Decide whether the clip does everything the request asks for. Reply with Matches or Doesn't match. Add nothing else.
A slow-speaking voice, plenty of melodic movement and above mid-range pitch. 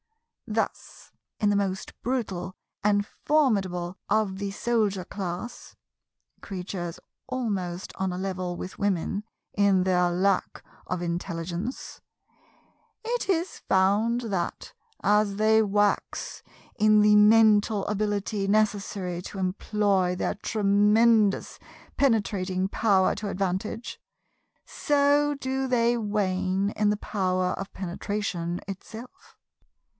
Doesn't match